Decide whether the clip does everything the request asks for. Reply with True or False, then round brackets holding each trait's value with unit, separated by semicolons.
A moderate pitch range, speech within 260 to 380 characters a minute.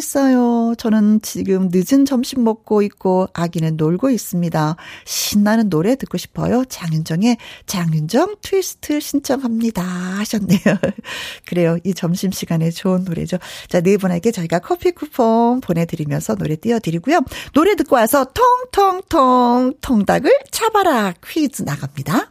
False (6.7 semitones; 310 characters per minute)